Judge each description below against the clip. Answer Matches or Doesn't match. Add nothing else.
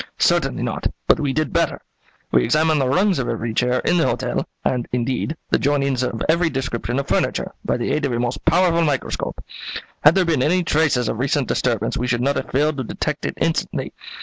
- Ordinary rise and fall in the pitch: Matches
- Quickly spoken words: Matches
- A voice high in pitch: Doesn't match